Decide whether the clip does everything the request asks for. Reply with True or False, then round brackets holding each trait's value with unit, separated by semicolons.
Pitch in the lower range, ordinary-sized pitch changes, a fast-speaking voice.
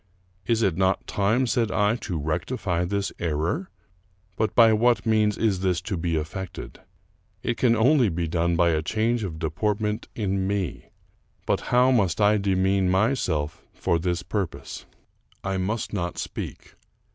False (100 Hz; 4.1 semitones; 155 wpm)